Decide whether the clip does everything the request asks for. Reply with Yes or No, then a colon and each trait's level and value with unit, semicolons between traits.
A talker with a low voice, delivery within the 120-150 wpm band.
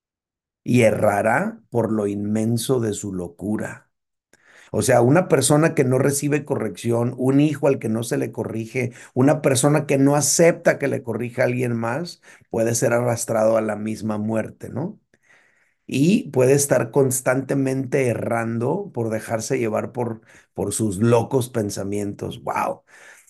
Yes: low, 120 Hz; average, 145 wpm